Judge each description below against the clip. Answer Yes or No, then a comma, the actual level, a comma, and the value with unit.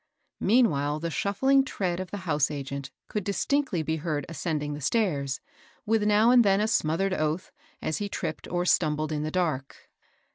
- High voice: No, medium, 170 Hz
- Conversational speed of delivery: Yes, average, 175 wpm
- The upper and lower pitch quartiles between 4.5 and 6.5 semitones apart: Yes, average, 5.3 semitones